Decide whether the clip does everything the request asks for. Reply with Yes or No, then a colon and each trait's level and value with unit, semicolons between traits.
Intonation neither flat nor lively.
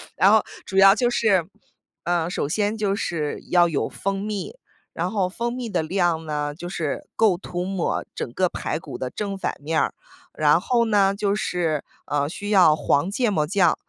Yes: average, 4.2 semitones